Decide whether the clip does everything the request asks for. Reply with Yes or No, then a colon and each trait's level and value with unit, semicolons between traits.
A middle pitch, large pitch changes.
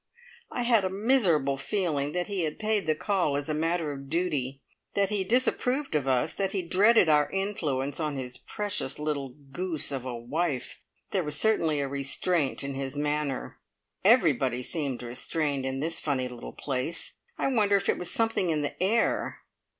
Yes: medium, 155 Hz; wide, 5.8 semitones